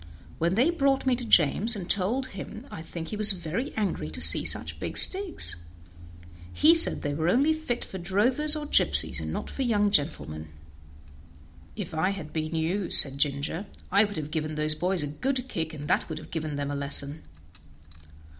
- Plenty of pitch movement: Yes, wide, 7.7 semitones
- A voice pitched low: No, medium, 185 Hz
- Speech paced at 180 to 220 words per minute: Yes, average, 190 wpm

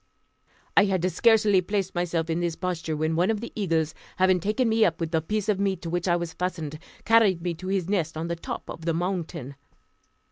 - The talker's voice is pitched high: No, medium, 175 Hz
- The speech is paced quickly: Yes, fast, 220 wpm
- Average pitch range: Yes, average, 3.1 semitones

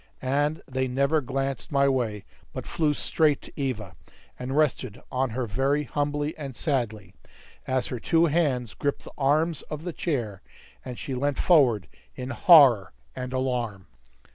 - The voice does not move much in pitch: No, average, 3.0 semitones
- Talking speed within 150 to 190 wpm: Yes, average, 155 wpm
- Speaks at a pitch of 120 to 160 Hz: Yes, low, 135 Hz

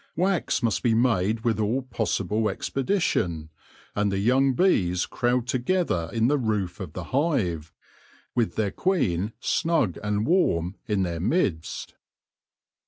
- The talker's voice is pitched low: Yes, low, 110 Hz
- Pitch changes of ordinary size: No, wide, 6.1 semitones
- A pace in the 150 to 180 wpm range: No, slow, 135 wpm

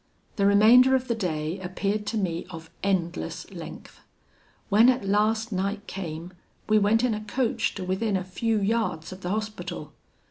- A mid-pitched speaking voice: No, high, 200 Hz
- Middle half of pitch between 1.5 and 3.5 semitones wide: Yes, average, 3.1 semitones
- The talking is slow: No, average, 170 wpm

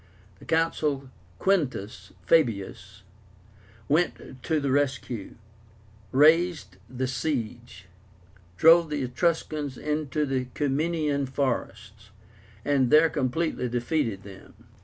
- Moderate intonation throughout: Yes, average, 4.2 semitones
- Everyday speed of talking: No, slow, 95 wpm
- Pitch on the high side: No, medium, 140 Hz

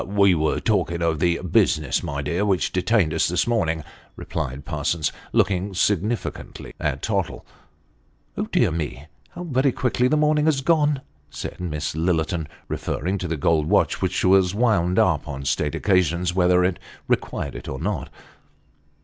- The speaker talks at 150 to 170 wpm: Yes, average, 160 wpm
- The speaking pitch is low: Yes, very low, 90 Hz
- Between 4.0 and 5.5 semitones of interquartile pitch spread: Yes, average, 4.4 semitones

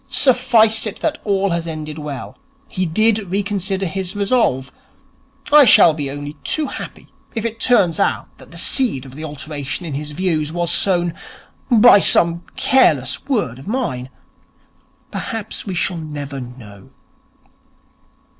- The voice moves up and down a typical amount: No, wide, 6.6 semitones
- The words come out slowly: No, average, 145 wpm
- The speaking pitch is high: No, medium, 175 Hz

